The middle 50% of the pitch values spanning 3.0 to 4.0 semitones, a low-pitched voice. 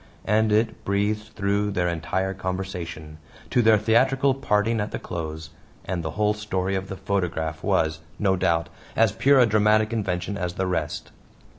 Yes: average, 3.3 semitones; low, 100 Hz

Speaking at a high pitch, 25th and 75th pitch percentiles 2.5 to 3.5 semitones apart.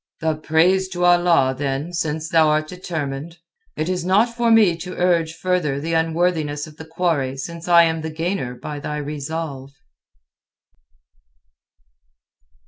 No: medium, 160 Hz; average, 2.9 semitones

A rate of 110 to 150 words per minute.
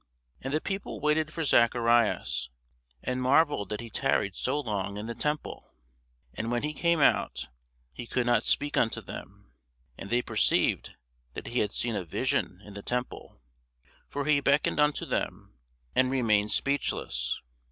No: average, 160 wpm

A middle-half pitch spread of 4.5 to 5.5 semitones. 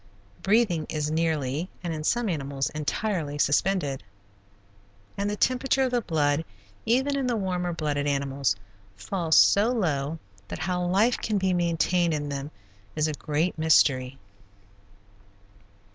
Yes: average, 5.2 semitones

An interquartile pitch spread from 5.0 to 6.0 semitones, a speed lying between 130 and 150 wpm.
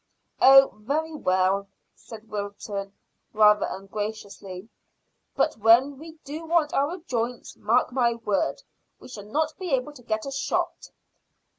Yes: average, 5.3 semitones; slow, 135 wpm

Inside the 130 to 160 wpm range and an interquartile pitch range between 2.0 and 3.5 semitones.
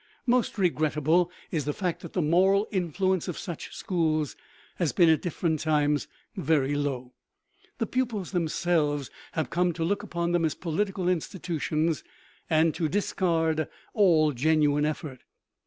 Yes: average, 140 wpm; average, 2.9 semitones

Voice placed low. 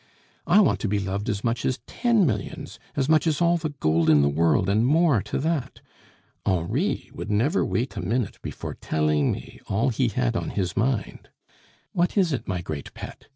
Yes: low, 115 Hz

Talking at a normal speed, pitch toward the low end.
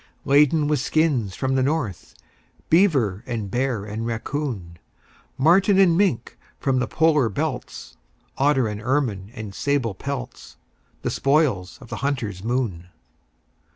No: slow, 130 wpm; low, 130 Hz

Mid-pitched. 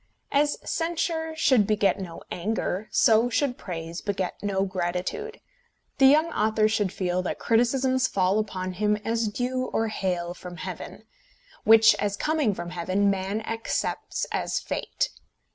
No: high, 215 Hz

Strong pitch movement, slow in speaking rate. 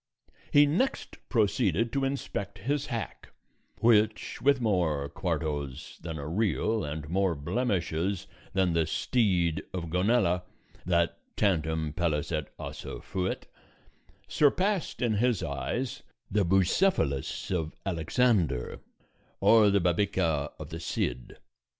Yes: wide, 6.1 semitones; slow, 115 wpm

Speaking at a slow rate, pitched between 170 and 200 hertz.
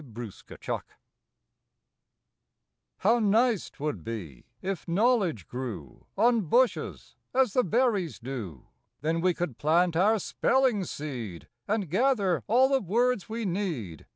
Yes: slow, 125 wpm; medium, 185 Hz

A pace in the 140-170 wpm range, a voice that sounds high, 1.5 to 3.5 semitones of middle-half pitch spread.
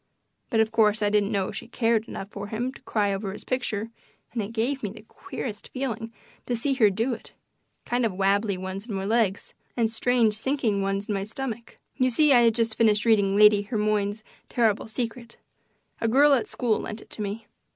No: fast, 205 wpm; high, 220 Hz; narrow, 2.6 semitones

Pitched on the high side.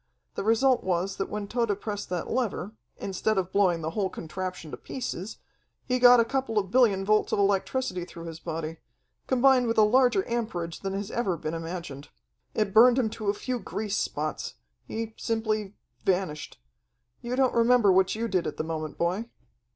Yes: high, 205 Hz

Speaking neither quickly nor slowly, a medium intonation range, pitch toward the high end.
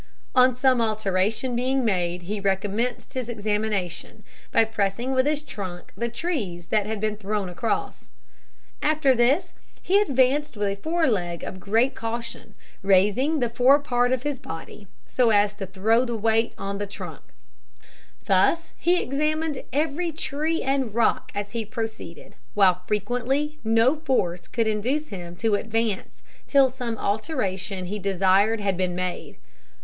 Yes: average, 150 wpm; average, 4.7 semitones; high, 225 Hz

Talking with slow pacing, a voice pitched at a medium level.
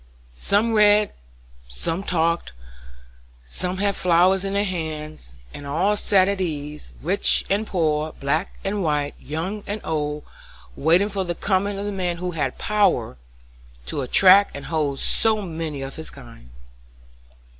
No: average, 145 wpm; medium, 175 Hz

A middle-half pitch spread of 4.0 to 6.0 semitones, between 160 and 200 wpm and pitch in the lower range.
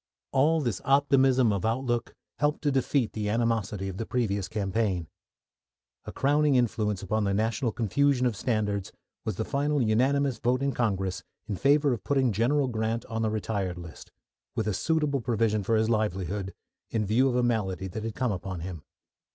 Yes: average, 4.4 semitones; average, 175 wpm; low, 115 Hz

